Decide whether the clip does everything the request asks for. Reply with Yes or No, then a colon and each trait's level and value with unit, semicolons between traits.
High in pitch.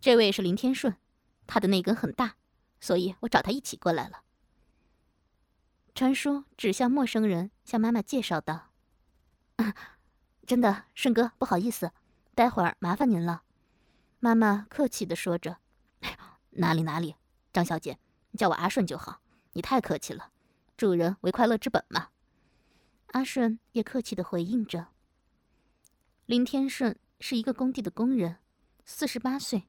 Yes: high, 230 Hz